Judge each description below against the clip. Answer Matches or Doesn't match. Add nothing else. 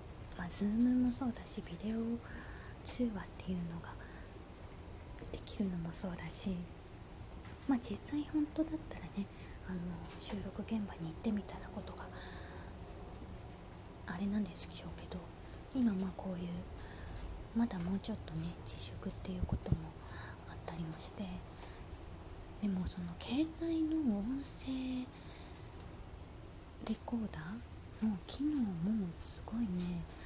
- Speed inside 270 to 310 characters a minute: Doesn't match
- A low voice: Matches